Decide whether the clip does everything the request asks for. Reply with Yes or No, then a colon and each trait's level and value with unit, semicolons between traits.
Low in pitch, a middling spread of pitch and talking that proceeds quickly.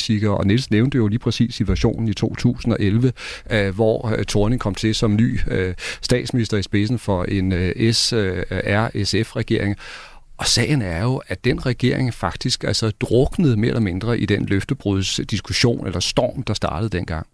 No: low, 110 Hz; average, 3.2 semitones; average, 150 wpm